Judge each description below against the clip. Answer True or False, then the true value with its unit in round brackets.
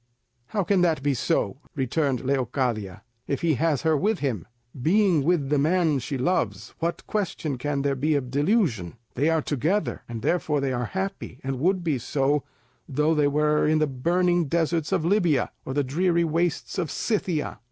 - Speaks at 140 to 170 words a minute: False (180 wpm)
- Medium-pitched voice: True (150 Hz)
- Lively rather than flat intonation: False (4.2 semitones)